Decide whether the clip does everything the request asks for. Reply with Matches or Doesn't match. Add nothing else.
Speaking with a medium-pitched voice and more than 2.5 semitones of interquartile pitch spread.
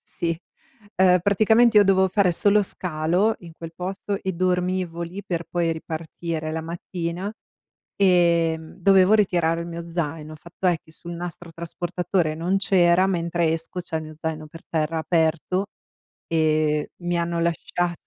Doesn't match